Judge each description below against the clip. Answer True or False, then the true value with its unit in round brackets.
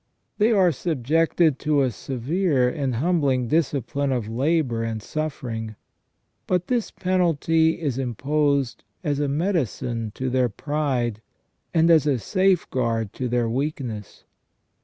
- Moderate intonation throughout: True (4.9 semitones)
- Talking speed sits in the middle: False (125 wpm)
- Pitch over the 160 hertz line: False (140 Hz)